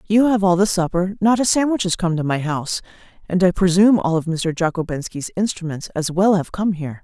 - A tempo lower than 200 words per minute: No, fast, 205 wpm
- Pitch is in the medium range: Yes, medium, 180 Hz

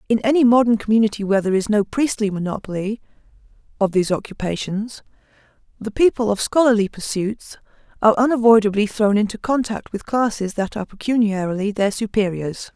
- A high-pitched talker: Yes, high, 215 Hz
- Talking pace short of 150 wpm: Yes, average, 140 wpm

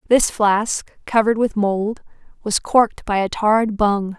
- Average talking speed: Yes, average, 160 wpm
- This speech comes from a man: No, female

